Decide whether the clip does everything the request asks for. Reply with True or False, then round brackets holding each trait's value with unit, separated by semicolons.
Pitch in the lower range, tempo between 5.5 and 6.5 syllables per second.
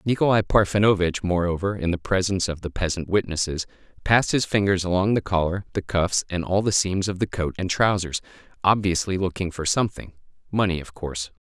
True (95 Hz; 5.8 syllables/s)